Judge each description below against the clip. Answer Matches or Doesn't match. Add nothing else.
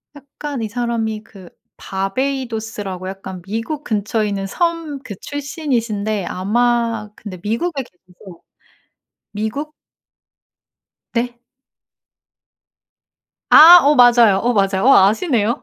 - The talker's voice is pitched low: Doesn't match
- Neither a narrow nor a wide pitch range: Matches